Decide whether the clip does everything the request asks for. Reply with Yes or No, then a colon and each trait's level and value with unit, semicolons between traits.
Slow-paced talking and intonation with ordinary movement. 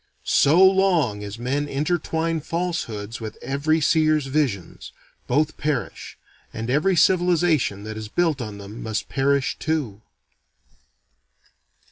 No: slow, 115 wpm; wide, 6.4 semitones